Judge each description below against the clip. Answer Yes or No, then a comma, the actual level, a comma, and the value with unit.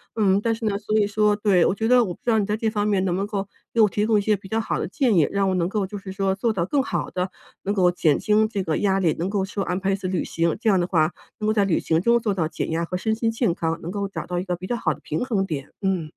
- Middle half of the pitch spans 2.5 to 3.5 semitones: Yes, average, 3.0 semitones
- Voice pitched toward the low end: No, high, 195 Hz